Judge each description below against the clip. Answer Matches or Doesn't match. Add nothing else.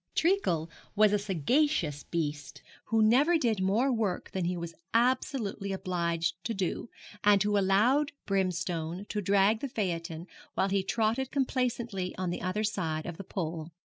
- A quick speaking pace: Doesn't match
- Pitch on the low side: Doesn't match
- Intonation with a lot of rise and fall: Doesn't match